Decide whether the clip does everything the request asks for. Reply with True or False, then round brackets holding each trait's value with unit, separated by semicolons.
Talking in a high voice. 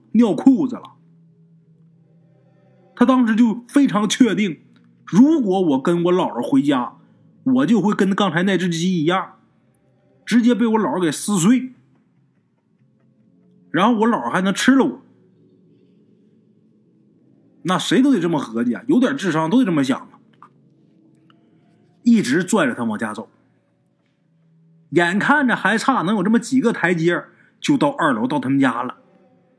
True (215 Hz)